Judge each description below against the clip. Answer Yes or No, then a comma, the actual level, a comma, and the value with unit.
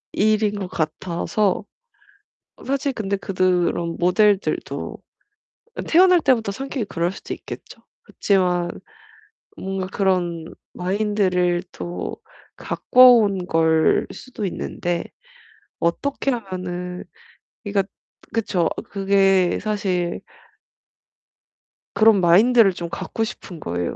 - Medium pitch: No, high, 195 Hz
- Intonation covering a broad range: No, average, 3.4 semitones